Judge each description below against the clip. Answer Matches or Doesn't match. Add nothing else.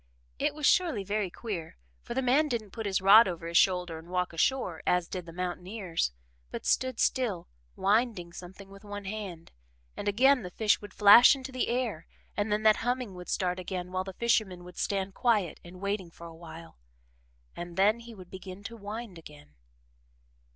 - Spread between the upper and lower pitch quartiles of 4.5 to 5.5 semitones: Doesn't match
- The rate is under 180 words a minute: Doesn't match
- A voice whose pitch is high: Matches